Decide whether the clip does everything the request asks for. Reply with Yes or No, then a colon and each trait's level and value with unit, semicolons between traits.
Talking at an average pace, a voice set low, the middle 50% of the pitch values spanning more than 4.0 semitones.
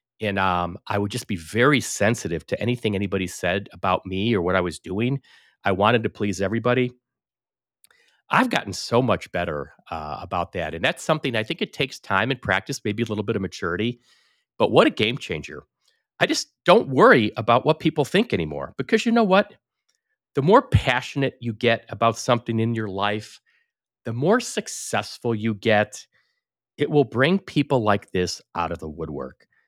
Yes: average, 185 wpm; low, 115 Hz; average, 5.0 semitones